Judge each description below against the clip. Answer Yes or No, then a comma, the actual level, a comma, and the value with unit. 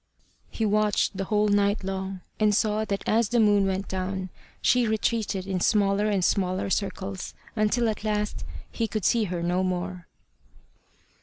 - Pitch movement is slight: Yes, narrow, 2.1 semitones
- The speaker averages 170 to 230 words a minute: No, average, 160 wpm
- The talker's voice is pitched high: Yes, high, 200 Hz